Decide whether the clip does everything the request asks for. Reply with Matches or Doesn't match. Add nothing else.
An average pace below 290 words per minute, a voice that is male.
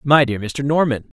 Matches